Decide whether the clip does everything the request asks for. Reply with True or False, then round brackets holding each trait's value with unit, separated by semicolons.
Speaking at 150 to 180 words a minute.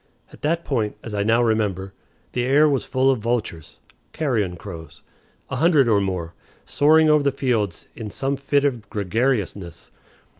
True (160 wpm)